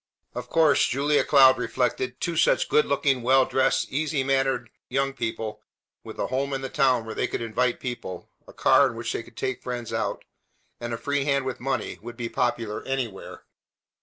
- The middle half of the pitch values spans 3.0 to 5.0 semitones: No, narrow, 2.4 semitones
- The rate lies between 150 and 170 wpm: No, average, 190 wpm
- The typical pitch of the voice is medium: No, low, 130 Hz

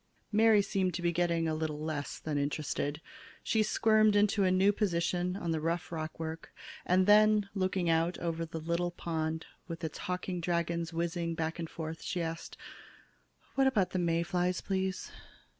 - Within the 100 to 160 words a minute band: No, average, 170 wpm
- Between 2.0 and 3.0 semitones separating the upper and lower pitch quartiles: Yes, narrow, 2.5 semitones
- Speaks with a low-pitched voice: No, medium, 170 Hz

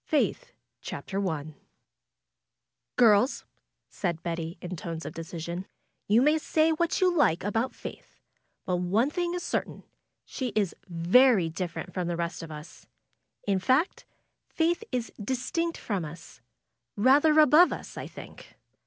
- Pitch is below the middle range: No, high, 205 Hz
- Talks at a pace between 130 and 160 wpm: Yes, average, 140 wpm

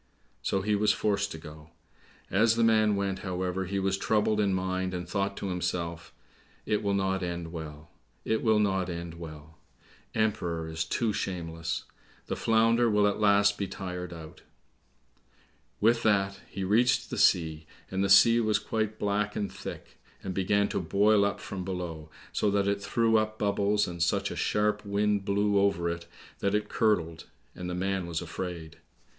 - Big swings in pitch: No, average, 3.0 semitones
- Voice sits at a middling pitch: No, low, 100 Hz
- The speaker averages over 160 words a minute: Yes, average, 175 wpm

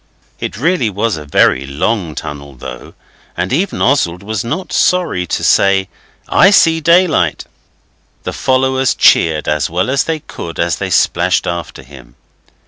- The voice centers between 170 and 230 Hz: No, very low, 95 Hz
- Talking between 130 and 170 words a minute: Yes, average, 150 wpm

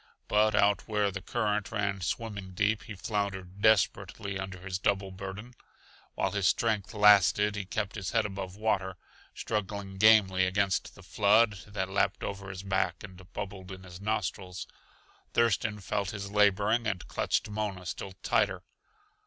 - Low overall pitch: Yes, low, 100 Hz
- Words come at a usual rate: Yes, average, 155 wpm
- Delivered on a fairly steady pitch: Yes, narrow, 1.8 semitones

